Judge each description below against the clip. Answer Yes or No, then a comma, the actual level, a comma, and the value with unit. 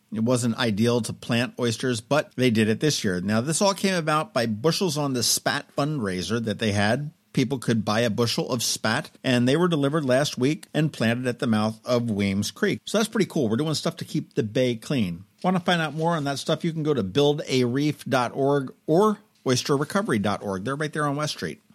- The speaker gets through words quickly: Yes, fast, 220 wpm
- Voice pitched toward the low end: Yes, low, 130 Hz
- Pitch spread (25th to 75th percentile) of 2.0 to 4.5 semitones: No, average, 5.1 semitones